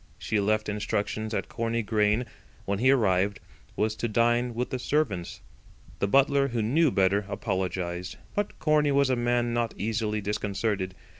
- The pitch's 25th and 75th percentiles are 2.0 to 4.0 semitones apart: Yes, average, 3.1 semitones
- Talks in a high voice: No, low, 110 Hz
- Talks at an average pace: Yes, average, 155 wpm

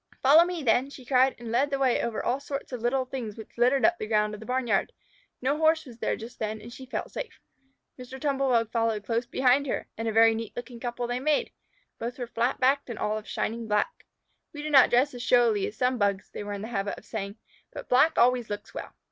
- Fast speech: Yes, fast, 245 wpm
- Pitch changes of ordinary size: Yes, average, 3.1 semitones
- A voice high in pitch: Yes, high, 245 Hz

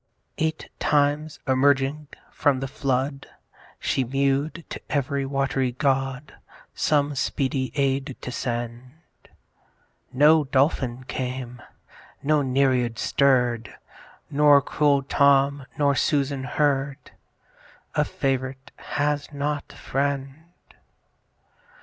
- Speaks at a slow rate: Yes, slow, 95 wpm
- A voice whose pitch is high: No, low, 135 Hz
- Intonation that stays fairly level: Yes, narrow, 1.6 semitones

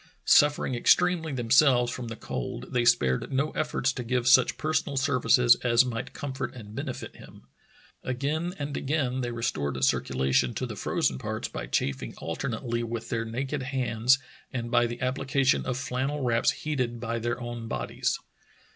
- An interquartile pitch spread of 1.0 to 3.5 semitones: Yes, average, 2.7 semitones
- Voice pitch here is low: Yes, low, 125 Hz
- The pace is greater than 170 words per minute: No, average, 160 wpm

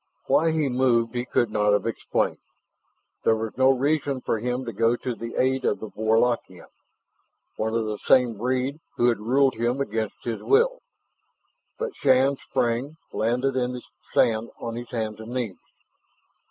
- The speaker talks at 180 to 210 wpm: No, average, 165 wpm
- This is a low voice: Yes, low, 120 Hz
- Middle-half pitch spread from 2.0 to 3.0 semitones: Yes, average, 2.7 semitones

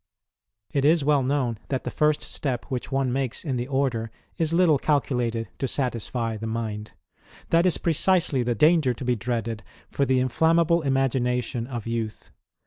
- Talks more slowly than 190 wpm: Yes, average, 165 wpm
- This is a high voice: No, low, 130 Hz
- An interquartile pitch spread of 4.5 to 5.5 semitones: No, average, 3.9 semitones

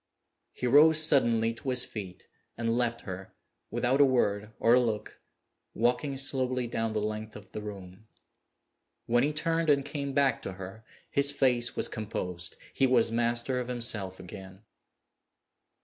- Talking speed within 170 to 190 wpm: No, average, 155 wpm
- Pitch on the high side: No, low, 120 Hz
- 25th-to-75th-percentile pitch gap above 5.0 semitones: No, average, 3.9 semitones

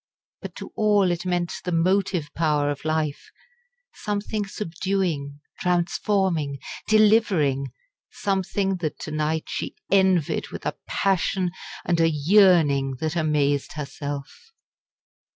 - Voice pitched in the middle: Yes, medium, 170 Hz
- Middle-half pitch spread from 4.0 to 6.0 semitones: Yes, average, 4.5 semitones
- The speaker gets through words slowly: Yes, slow, 115 wpm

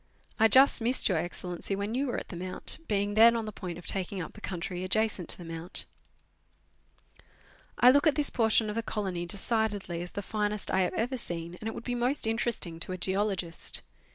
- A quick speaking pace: Yes, fast, 210 wpm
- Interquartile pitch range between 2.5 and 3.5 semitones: No, average, 4.0 semitones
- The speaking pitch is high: Yes, high, 205 Hz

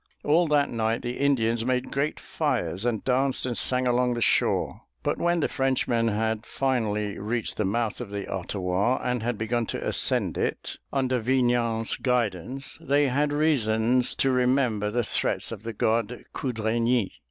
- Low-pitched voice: Yes, low, 120 Hz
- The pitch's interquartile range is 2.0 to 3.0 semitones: Yes, average, 2.7 semitones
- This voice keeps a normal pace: Yes, average, 165 wpm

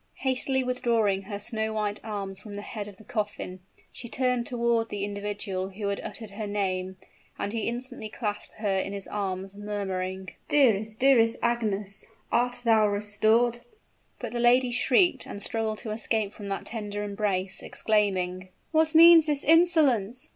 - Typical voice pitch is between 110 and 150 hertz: No, high, 215 Hz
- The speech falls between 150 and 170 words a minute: Yes, average, 160 wpm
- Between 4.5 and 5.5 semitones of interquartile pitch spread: No, average, 3.1 semitones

